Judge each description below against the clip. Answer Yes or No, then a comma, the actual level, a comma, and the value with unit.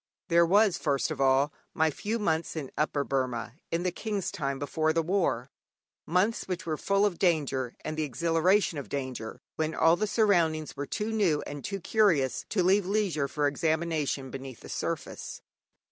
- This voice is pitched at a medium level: Yes, medium, 160 Hz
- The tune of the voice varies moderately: Yes, average, 4.9 semitones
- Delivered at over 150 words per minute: Yes, average, 175 wpm